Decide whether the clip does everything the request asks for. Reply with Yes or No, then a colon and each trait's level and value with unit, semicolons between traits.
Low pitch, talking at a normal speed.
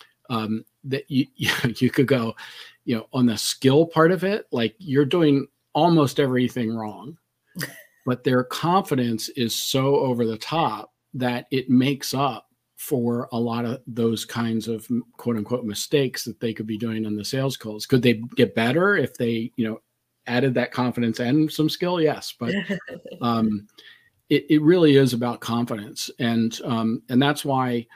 Yes: low, 125 Hz; average, 170 wpm